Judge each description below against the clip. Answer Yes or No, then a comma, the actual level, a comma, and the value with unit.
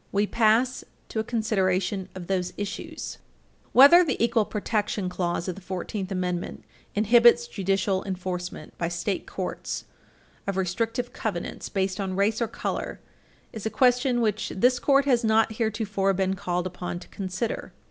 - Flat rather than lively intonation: No, average, 3.5 semitones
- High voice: Yes, high, 200 Hz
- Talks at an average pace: Yes, average, 155 wpm